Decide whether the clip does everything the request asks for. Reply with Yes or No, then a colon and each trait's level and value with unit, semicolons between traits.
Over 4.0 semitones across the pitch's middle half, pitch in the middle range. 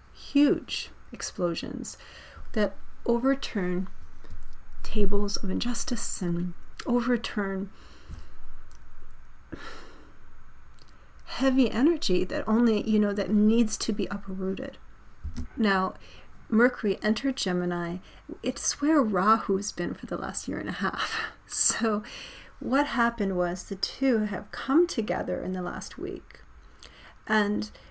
No: average, 4.9 semitones; high, 210 Hz